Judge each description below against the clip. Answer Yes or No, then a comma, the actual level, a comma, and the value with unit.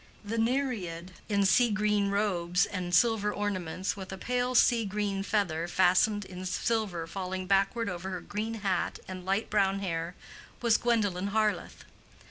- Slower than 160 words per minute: Yes, average, 150 wpm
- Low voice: No, high, 200 Hz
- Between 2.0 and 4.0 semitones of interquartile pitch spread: Yes, average, 2.8 semitones